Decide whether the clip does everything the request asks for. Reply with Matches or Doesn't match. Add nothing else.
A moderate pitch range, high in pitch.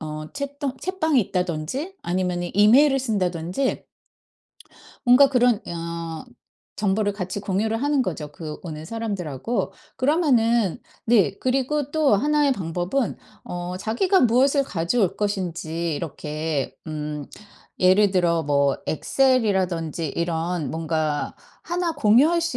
Doesn't match